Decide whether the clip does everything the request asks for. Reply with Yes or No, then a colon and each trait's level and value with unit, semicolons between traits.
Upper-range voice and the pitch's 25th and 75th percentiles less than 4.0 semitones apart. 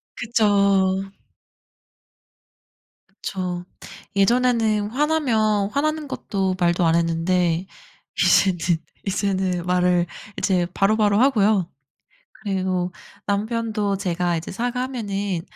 Yes: high, 195 Hz; average, 3.4 semitones